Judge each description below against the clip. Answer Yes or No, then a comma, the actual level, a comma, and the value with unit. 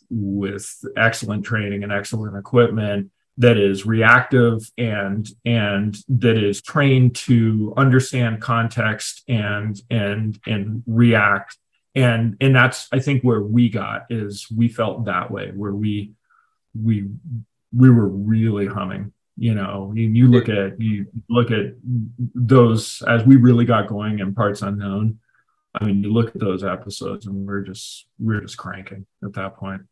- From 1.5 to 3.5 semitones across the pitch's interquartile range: Yes, average, 2.8 semitones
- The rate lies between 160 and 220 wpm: No, average, 150 wpm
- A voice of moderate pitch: No, low, 110 Hz